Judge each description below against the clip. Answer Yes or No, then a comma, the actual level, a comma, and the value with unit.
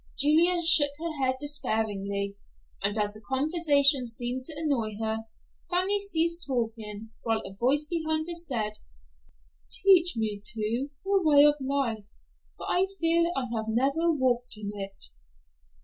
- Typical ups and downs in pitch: No, wide, 6.7 semitones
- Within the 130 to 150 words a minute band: Yes, average, 145 wpm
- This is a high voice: Yes, very high, 265 Hz